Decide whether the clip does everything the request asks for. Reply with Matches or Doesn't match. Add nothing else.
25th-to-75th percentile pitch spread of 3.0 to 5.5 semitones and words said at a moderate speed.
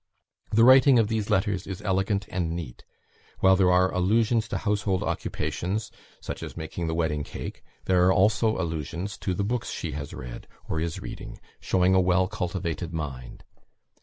Matches